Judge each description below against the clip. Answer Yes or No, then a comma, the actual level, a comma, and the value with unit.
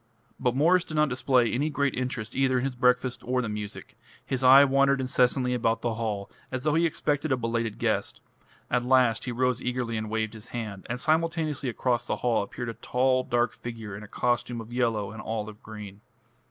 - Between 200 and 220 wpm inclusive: Yes, fast, 205 wpm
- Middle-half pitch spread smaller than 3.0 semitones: Yes, narrow, 2.6 semitones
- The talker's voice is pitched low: Yes, low, 125 Hz